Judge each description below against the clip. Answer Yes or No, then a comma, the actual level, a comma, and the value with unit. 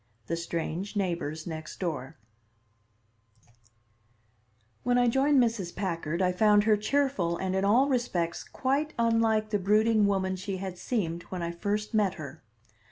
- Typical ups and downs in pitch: Yes, average, 4.8 semitones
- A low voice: No, high, 200 Hz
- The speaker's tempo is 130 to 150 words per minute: Yes, average, 145 wpm